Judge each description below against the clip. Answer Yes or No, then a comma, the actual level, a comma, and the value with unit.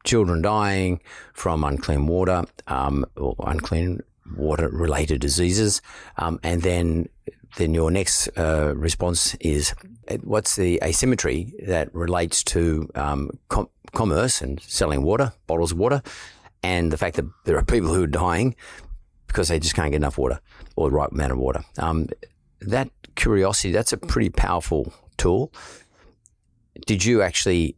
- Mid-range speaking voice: No, very low, 85 Hz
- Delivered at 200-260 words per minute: No, average, 150 wpm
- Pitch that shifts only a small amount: No, average, 3.0 semitones